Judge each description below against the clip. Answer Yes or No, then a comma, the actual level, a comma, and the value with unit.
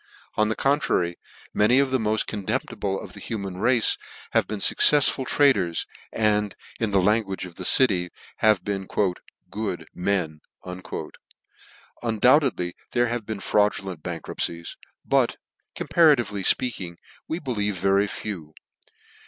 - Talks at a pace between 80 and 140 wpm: Yes, slow, 135 wpm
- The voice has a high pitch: No, low, 105 Hz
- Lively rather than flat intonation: No, average, 4.2 semitones